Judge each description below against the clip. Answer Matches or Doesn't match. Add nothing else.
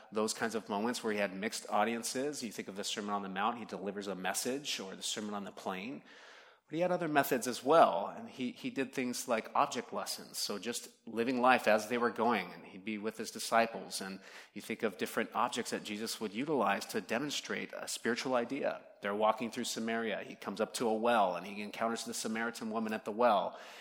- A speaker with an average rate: Doesn't match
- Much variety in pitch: Doesn't match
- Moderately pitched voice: Doesn't match